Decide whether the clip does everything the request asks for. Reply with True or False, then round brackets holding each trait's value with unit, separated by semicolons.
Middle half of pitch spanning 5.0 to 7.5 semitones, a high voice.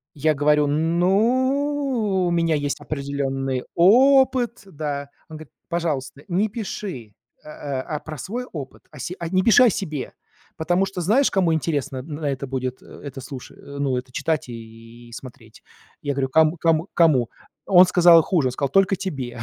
False (5.5 semitones; 155 Hz)